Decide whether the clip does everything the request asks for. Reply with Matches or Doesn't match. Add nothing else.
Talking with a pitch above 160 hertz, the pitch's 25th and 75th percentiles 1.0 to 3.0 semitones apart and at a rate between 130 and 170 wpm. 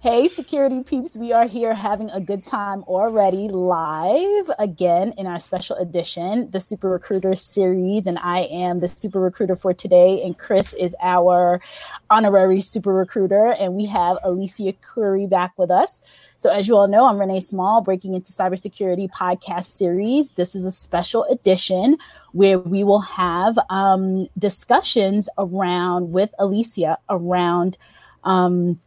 Matches